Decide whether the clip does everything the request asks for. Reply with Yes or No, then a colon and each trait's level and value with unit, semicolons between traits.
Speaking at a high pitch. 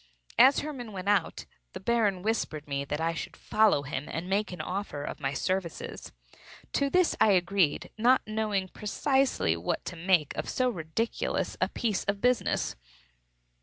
Yes: high, 195 Hz